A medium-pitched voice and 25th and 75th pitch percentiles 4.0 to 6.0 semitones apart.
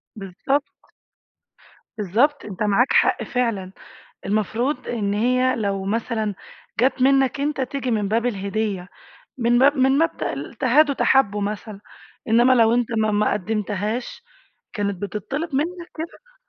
No: high, 230 Hz; average, 4.4 semitones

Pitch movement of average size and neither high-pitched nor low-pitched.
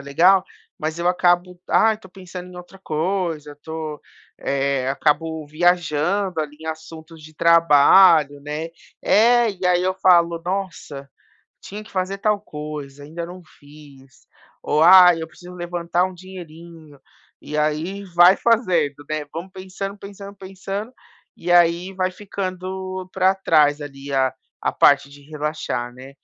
Yes: average, 3.7 semitones; medium, 170 Hz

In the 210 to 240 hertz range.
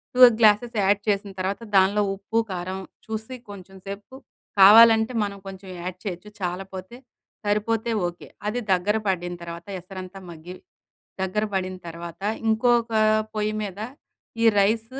No: high, 200 Hz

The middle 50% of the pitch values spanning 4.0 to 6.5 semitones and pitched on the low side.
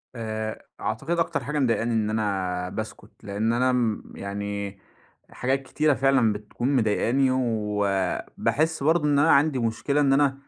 Yes: average, 4.6 semitones; low, 115 Hz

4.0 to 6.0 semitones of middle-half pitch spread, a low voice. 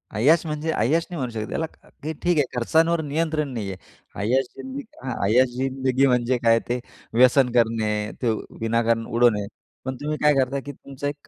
Yes: average, 4.4 semitones; low, 130 Hz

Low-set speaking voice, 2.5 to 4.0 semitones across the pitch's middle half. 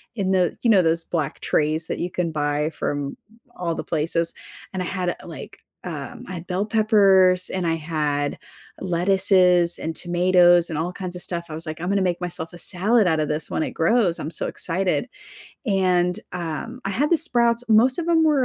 No: medium, 180 Hz; average, 3.1 semitones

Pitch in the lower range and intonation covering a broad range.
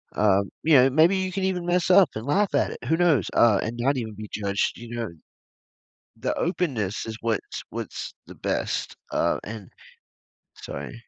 Yes: low, 120 Hz; wide, 8.2 semitones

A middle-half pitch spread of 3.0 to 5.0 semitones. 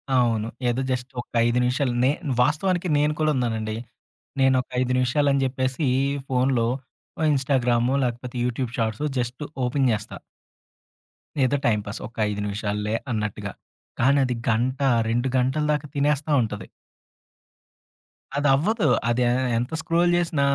Yes: average, 3.3 semitones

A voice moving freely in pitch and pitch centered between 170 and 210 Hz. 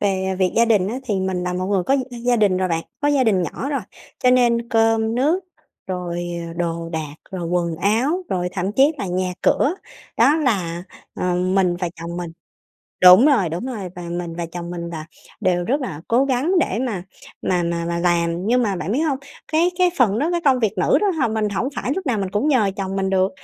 Yes: wide, 5.8 semitones; high, 195 Hz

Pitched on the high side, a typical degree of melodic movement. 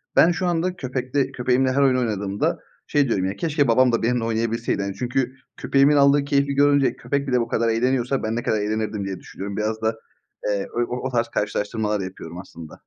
No: low, 120 Hz; average, 4.2 semitones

